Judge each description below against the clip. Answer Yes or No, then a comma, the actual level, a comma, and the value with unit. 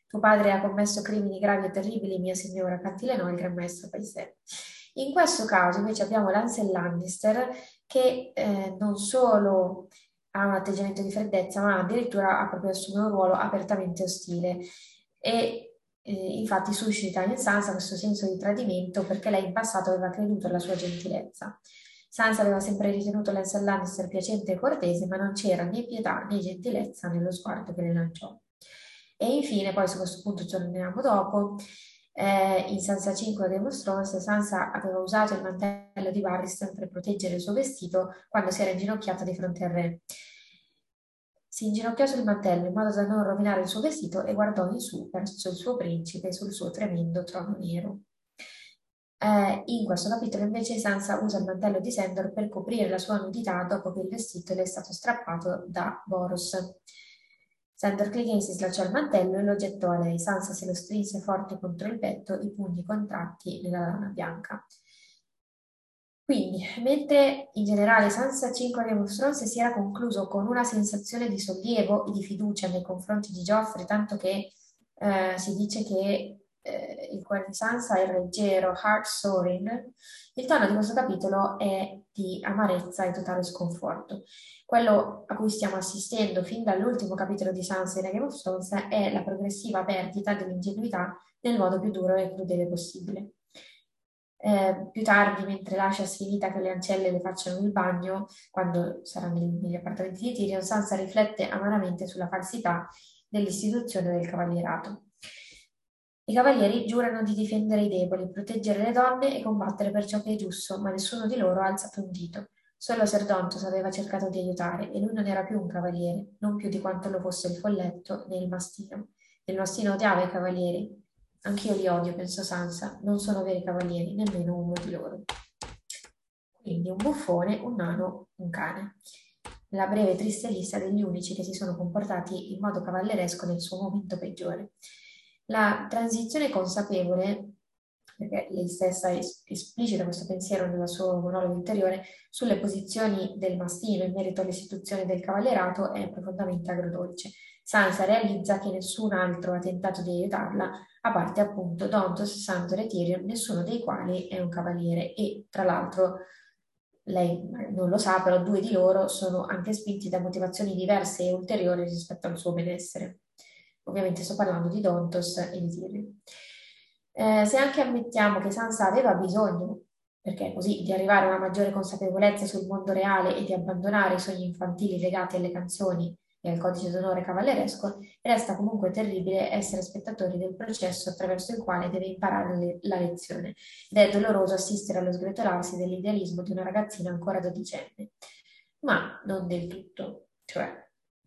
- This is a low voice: No, high, 195 Hz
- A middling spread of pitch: No, narrow, 2.2 semitones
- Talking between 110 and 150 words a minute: No, average, 165 wpm